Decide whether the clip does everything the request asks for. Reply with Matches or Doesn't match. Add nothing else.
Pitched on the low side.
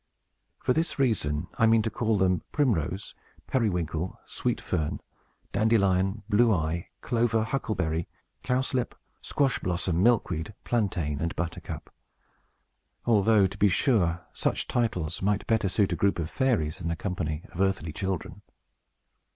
Matches